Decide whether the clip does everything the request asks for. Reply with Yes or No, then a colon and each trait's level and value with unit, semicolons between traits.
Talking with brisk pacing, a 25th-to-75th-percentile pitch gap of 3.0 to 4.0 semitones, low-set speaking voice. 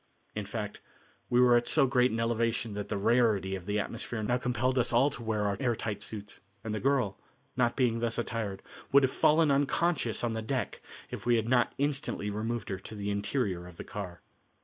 Yes: fast, 215 wpm; average, 3.3 semitones; low, 115 Hz